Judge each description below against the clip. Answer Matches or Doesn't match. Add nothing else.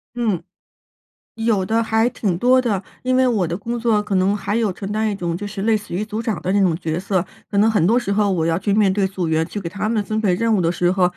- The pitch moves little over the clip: Doesn't match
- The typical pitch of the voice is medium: Doesn't match